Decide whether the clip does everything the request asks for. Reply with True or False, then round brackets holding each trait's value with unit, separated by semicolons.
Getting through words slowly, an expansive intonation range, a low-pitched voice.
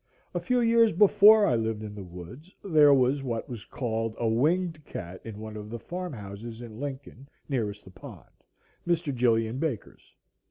False (175 wpm; 6.4 semitones; 120 Hz)